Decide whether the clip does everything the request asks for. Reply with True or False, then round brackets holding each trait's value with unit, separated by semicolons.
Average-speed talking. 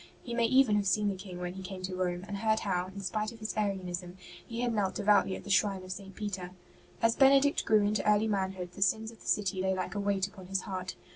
False (260 wpm)